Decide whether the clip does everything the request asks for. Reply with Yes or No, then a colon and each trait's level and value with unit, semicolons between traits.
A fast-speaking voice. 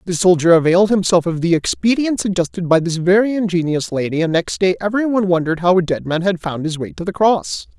Yes: fast, 225 wpm